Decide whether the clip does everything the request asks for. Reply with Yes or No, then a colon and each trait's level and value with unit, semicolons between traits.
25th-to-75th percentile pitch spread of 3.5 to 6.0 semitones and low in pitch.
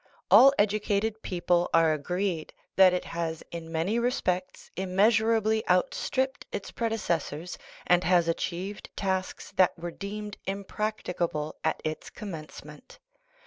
No: average, 3.8 semitones; medium, 185 Hz